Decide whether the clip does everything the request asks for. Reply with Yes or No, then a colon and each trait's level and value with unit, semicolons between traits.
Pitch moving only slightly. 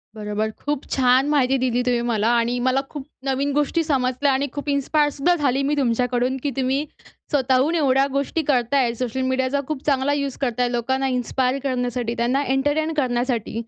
Yes: narrow, 2.3 semitones